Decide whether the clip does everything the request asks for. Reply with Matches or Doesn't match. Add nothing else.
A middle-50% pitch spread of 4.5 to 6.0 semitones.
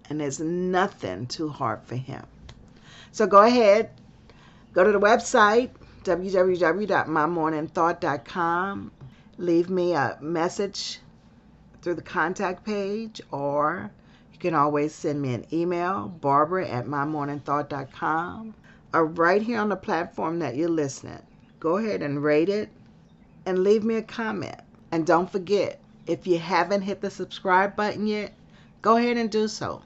Matches